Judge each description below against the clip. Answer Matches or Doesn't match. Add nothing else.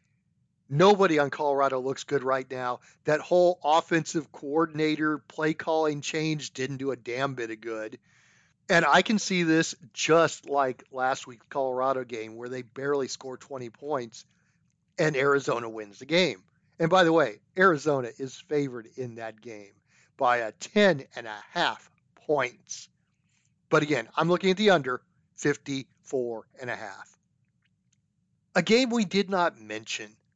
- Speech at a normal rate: Matches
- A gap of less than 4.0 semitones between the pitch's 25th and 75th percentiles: Doesn't match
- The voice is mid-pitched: Matches